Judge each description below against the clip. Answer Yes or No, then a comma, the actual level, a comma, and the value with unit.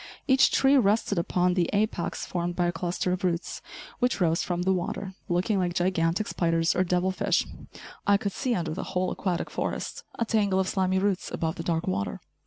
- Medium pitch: Yes, medium, 180 Hz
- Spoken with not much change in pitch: Yes, narrow, 2.3 semitones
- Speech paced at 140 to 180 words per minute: No, average, 195 wpm